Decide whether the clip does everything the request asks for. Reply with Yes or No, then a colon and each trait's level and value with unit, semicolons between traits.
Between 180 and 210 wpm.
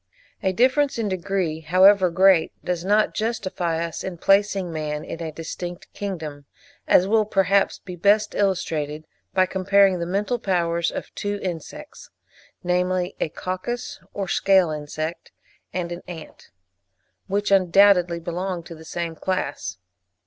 No: average, 140 wpm